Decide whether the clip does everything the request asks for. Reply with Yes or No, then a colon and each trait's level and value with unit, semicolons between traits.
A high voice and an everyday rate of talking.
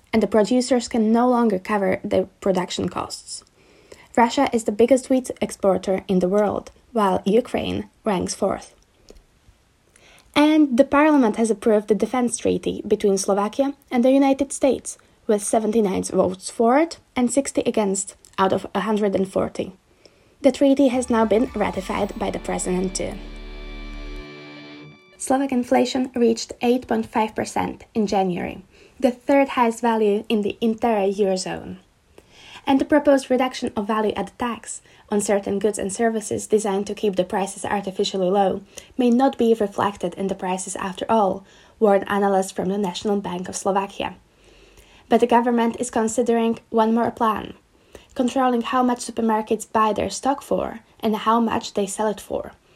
Yes: high, 220 Hz; average, 150 wpm